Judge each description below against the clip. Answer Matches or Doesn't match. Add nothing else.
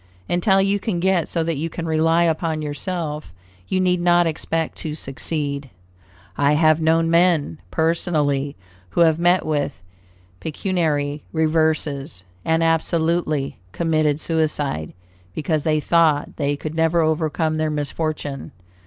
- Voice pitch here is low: Doesn't match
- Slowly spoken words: Matches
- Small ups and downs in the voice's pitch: Matches